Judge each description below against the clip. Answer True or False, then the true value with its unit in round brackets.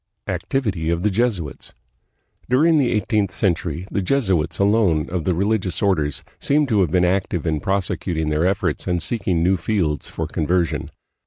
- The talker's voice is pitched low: True (95 Hz)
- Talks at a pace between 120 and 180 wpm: True (160 wpm)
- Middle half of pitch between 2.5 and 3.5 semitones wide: False (4.1 semitones)